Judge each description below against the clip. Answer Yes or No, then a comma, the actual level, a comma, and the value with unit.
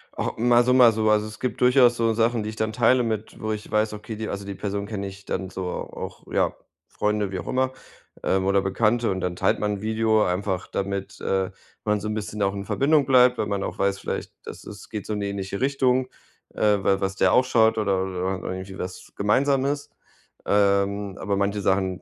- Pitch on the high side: No, low, 105 Hz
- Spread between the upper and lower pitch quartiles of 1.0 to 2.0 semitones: No, narrow, 2.6 semitones